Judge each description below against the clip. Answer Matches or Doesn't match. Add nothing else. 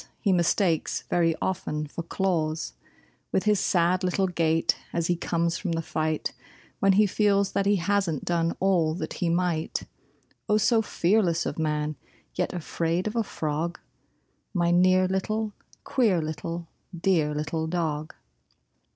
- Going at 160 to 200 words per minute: Doesn't match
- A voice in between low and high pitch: Matches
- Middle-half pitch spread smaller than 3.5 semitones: Matches